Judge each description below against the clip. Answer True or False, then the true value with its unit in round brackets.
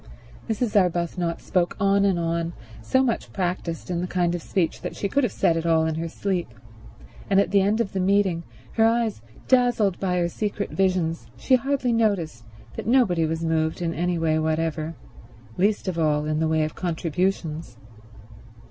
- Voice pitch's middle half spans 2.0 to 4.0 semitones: True (3.5 semitones)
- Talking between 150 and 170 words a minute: False (185 wpm)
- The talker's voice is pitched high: False (175 Hz)